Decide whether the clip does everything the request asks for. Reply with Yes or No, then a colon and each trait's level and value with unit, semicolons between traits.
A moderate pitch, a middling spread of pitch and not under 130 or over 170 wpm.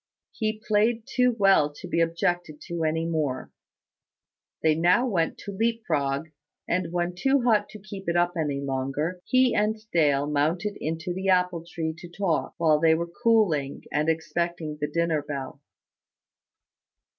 Yes: medium, 170 Hz; average, 4.1 semitones; average, 155 wpm